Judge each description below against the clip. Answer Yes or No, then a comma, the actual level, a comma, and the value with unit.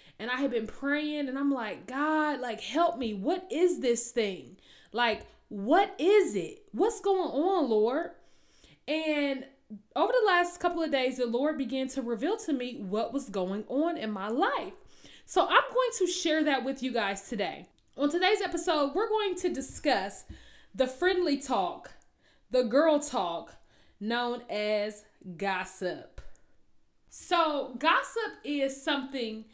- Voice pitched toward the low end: No, very high, 275 Hz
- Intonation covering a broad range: Yes, wide, 6.4 semitones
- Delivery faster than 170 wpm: No, average, 150 wpm